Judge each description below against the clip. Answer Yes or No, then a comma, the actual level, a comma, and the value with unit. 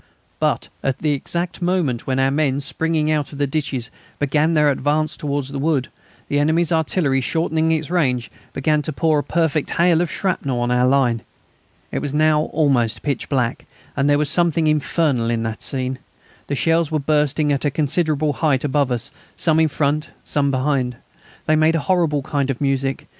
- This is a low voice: No, medium, 145 Hz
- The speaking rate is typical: Yes, average, 185 wpm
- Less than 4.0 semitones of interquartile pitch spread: Yes, average, 2.7 semitones